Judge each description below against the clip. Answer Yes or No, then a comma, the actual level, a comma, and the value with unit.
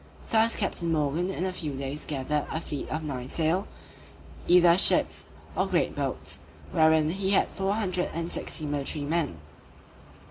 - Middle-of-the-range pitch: Yes, medium, 160 Hz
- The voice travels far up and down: No, average, 3.7 semitones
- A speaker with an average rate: Yes, average, 155 wpm